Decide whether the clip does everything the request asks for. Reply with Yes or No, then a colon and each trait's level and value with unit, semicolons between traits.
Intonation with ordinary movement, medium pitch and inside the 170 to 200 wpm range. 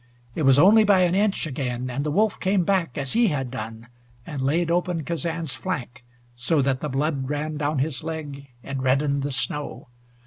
Yes: average, 4.1 semitones; medium, 150 Hz; average, 195 wpm